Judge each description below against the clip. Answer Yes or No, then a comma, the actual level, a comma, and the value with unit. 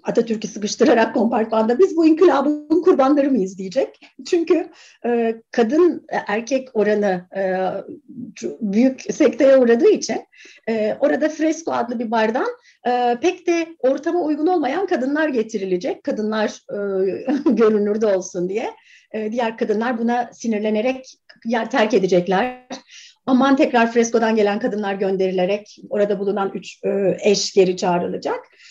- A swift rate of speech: No, average, 125 wpm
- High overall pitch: Yes, high, 235 Hz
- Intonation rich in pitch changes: Yes, wide, 6.0 semitones